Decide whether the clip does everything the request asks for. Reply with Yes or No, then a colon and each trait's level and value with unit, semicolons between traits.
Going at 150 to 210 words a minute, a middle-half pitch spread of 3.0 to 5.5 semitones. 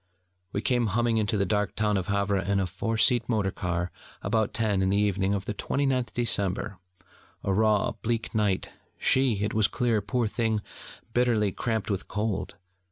No: average, 175 wpm; narrow, 2.4 semitones